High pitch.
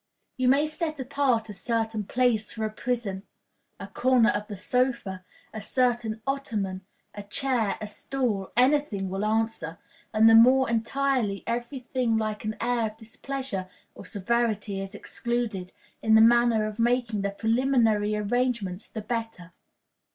Yes: high, 225 Hz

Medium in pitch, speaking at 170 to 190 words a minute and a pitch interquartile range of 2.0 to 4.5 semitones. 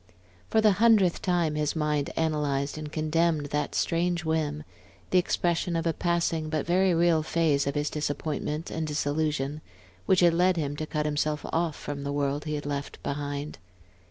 Yes: medium, 155 Hz; average, 175 wpm; narrow, 2.4 semitones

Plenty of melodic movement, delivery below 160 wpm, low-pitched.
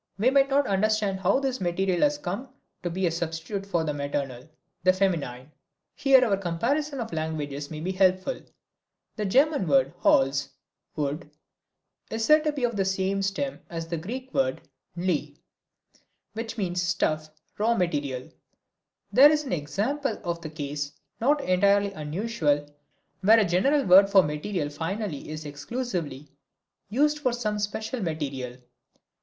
No: wide, 6.7 semitones; average, 150 wpm; high, 190 Hz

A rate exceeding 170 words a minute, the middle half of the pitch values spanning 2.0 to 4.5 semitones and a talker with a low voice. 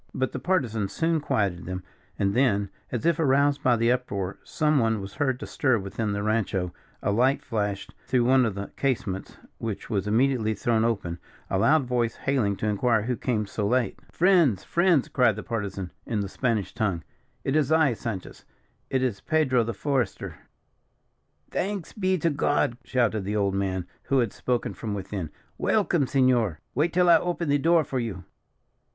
No: average, 180 wpm; average, 5.3 semitones; low, 120 Hz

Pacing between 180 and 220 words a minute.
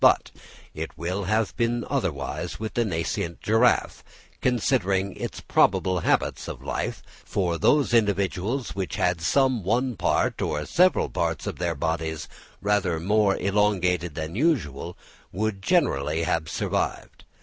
No: slow, 135 wpm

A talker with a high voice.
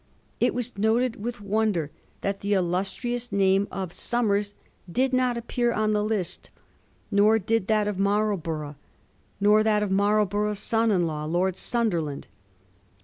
Yes: high, 210 Hz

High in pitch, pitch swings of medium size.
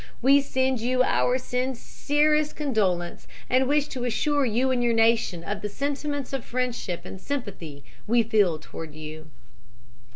Yes: high, 245 Hz; average, 5.0 semitones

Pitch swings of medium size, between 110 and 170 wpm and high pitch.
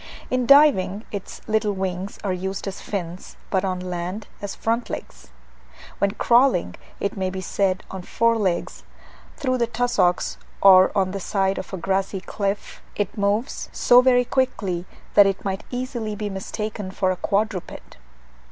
Yes: average, 3.3 semitones; average, 160 wpm; high, 200 Hz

